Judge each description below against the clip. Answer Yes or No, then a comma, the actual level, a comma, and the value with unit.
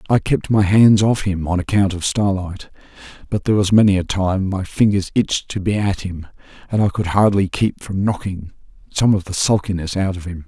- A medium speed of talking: No, fast, 210 wpm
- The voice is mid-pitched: No, very low, 95 Hz